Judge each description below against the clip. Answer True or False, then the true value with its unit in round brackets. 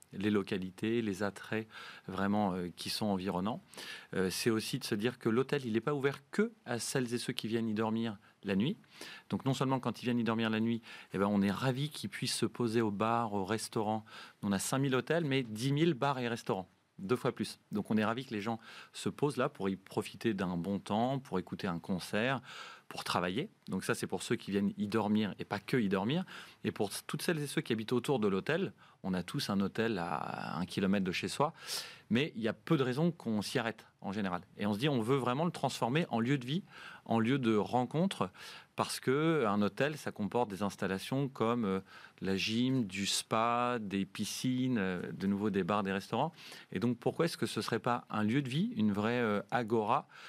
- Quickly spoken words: True (230 wpm)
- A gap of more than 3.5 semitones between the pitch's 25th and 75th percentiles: True (4.2 semitones)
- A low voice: True (115 Hz)